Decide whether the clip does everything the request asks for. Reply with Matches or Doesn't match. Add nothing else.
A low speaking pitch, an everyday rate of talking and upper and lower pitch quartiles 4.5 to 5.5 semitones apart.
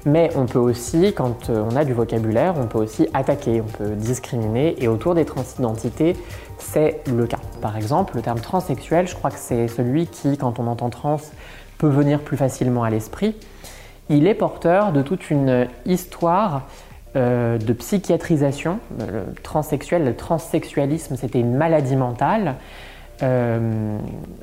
Matches